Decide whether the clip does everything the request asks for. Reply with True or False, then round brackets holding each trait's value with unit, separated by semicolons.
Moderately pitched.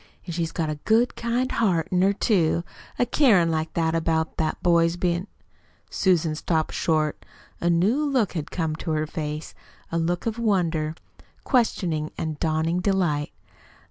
True (170 Hz)